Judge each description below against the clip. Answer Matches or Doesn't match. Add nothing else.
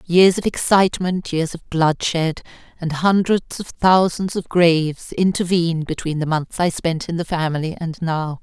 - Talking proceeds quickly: Doesn't match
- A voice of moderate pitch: Matches